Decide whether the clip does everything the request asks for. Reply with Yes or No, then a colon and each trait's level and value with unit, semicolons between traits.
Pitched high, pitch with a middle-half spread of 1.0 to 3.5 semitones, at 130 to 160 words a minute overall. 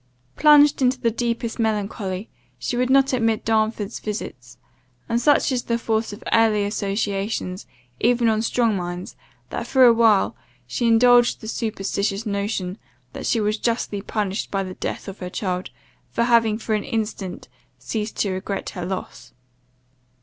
Yes: high, 220 Hz; average, 2.9 semitones; average, 155 wpm